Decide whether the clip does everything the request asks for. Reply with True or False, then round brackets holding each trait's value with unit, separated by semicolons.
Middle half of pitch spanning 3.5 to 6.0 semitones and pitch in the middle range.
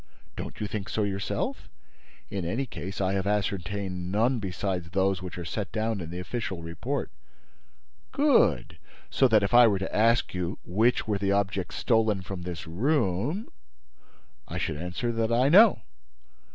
False (3.8 semitones; 100 Hz)